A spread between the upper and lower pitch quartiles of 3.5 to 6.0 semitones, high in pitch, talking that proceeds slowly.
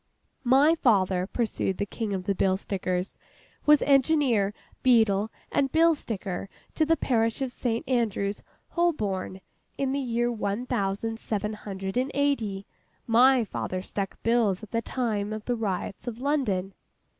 No: average, 4.6 semitones; high, 225 Hz; average, 150 wpm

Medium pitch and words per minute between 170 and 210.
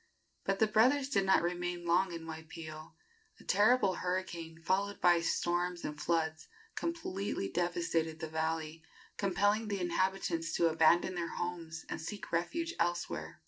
No: medium, 175 Hz; average, 145 wpm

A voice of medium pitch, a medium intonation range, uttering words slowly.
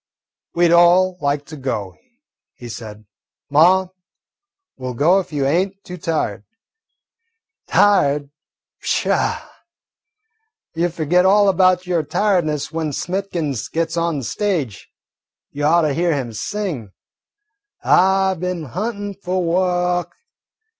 Yes: medium, 170 Hz; average, 4.3 semitones; slow, 125 wpm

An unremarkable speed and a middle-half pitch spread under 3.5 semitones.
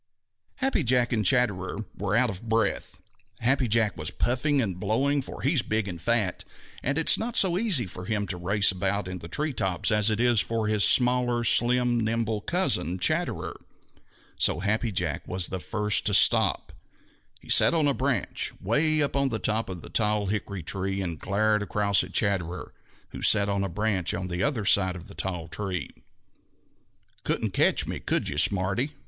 No: average, 190 wpm; average, 4.5 semitones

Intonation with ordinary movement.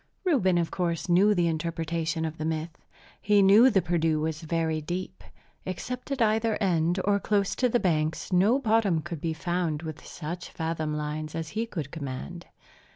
Yes: average, 3.9 semitones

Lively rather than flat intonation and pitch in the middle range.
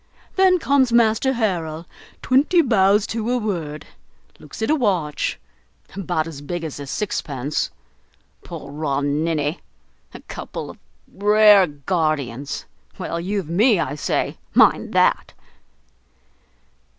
Yes: wide, 6.5 semitones; medium, 175 Hz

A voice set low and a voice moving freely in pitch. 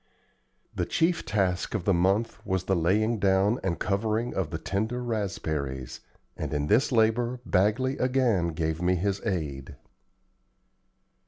No: low, 100 Hz; average, 4.3 semitones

